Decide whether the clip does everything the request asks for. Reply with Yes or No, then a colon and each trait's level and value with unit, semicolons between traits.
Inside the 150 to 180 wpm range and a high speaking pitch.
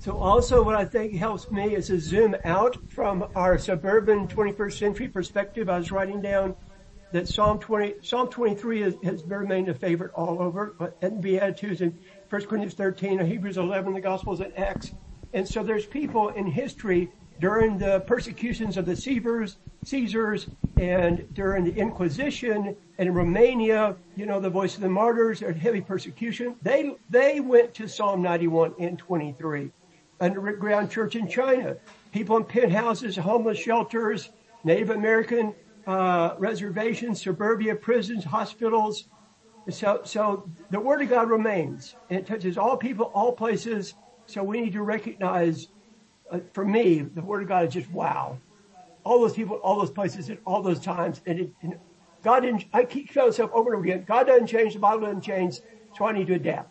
Yes: average, 175 wpm; high, 205 Hz